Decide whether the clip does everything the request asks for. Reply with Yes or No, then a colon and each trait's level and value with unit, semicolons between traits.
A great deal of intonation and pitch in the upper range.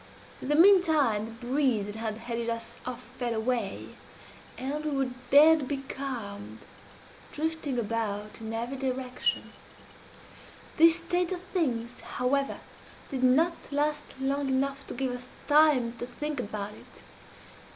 No: average, 4.1 semitones; very high, 260 Hz